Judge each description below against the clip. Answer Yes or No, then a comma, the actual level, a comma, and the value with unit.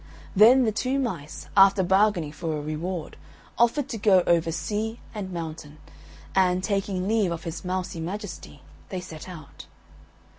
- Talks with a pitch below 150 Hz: No, medium, 185 Hz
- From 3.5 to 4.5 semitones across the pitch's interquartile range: Yes, average, 4.0 semitones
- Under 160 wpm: Yes, average, 150 wpm